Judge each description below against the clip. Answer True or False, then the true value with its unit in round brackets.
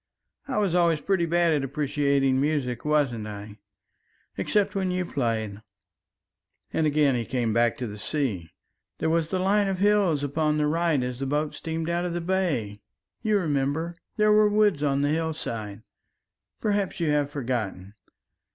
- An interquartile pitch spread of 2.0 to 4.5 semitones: False (5.3 semitones)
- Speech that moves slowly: False (165 wpm)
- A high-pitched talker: False (150 Hz)